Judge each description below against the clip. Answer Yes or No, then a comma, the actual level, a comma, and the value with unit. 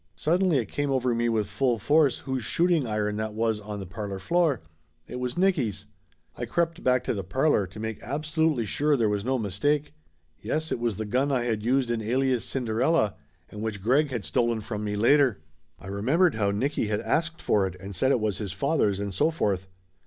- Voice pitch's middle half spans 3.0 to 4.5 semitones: No, wide, 5.4 semitones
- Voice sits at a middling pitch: No, low, 120 Hz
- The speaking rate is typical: No, fast, 210 wpm